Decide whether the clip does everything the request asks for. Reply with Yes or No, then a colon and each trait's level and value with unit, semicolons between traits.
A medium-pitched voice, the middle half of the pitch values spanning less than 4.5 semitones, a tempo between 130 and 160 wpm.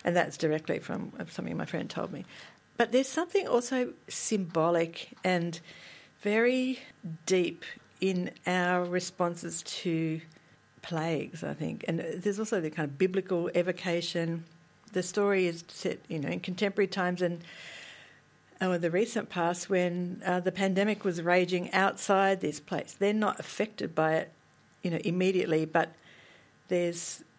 Yes: medium, 180 Hz; narrow, 2.4 semitones; average, 145 wpm